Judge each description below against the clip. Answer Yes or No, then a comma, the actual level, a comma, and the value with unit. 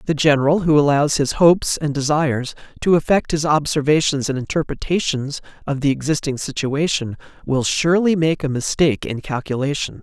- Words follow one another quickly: No, average, 150 wpm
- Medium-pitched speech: Yes, medium, 145 Hz